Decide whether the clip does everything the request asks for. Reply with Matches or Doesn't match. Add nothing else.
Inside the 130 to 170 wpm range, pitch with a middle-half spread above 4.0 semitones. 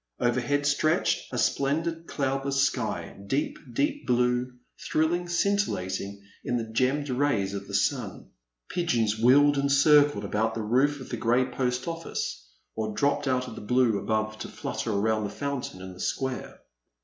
Matches